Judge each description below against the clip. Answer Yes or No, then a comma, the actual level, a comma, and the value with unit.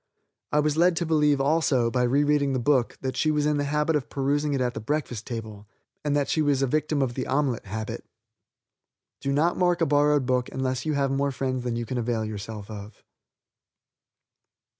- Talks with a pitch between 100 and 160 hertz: Yes, low, 135 Hz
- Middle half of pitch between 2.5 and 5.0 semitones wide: Yes, average, 3.4 semitones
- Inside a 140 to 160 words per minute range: No, fast, 205 wpm